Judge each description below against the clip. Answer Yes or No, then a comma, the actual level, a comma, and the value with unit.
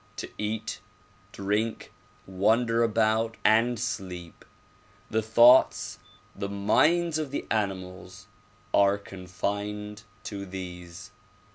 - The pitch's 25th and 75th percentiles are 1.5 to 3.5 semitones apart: Yes, average, 2.9 semitones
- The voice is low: Yes, low, 105 Hz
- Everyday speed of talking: No, slow, 100 wpm